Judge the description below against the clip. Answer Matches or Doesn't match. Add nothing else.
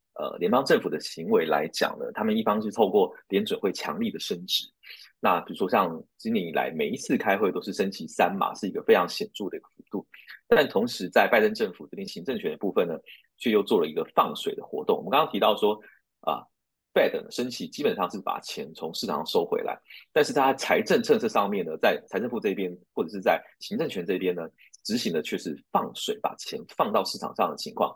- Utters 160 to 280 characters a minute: Doesn't match